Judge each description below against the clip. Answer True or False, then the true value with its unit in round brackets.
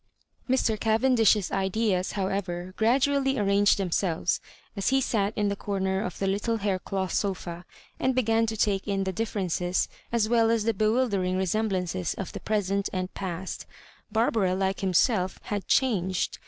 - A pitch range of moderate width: True (3.0 semitones)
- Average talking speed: True (155 wpm)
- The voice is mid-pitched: False (200 Hz)